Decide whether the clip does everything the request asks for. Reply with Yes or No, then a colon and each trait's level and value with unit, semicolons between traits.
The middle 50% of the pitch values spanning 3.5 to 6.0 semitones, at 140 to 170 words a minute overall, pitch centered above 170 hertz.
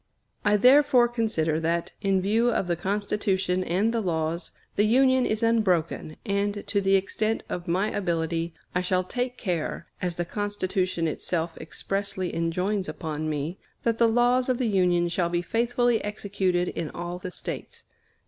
Yes: average, 4.1 semitones; average, 160 wpm; high, 190 Hz